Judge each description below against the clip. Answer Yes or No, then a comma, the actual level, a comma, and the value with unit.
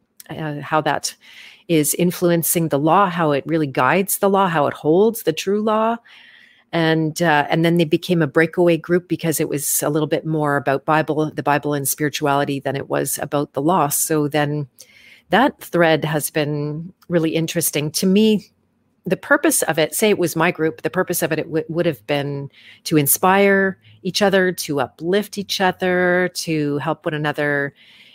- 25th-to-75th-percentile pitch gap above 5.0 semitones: No, average, 3.3 semitones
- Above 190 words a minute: No, average, 185 wpm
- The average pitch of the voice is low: No, medium, 160 Hz